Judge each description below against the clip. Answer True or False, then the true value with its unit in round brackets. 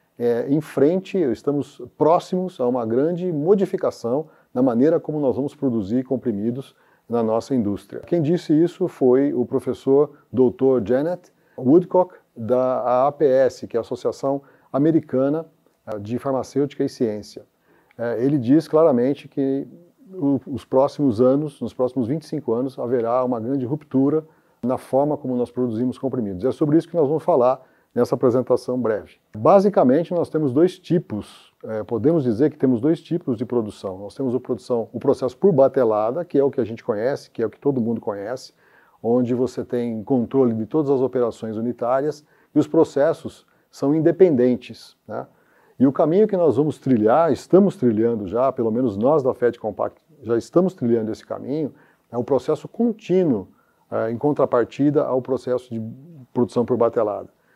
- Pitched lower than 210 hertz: True (135 Hz)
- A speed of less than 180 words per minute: True (165 wpm)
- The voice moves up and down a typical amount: True (4.4 semitones)